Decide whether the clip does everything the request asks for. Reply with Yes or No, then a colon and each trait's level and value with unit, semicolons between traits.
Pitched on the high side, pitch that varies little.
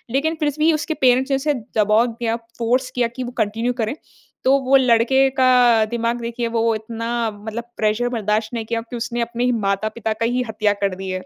Yes: high, 235 Hz; narrow, 2.3 semitones